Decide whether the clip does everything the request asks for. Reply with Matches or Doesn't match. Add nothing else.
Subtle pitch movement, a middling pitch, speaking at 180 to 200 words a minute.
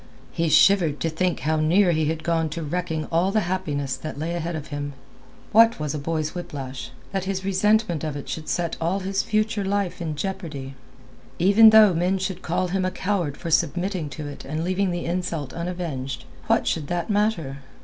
Doesn't match